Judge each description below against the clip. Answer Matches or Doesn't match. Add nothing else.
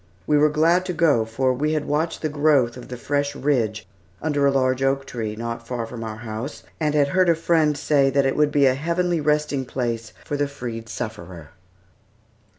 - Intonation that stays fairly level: Doesn't match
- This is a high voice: Doesn't match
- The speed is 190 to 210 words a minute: Matches